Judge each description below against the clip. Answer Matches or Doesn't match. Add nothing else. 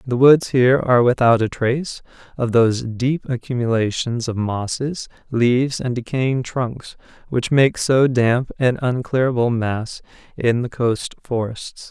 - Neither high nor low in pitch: Doesn't match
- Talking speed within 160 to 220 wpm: Doesn't match